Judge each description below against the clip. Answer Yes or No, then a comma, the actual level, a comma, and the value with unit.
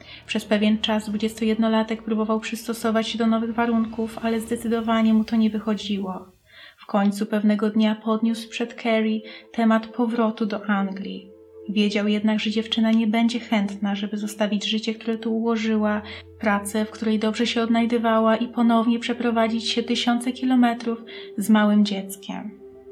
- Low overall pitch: No, high, 220 Hz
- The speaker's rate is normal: Yes, average, 145 wpm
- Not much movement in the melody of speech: Yes, narrow, 1.3 semitones